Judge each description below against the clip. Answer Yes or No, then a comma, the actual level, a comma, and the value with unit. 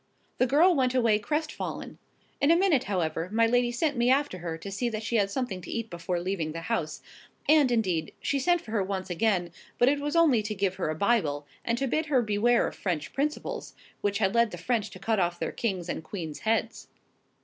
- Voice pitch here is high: Yes, high, 220 Hz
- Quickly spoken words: Yes, fast, 225 wpm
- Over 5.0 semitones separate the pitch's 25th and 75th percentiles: Yes, wide, 5.6 semitones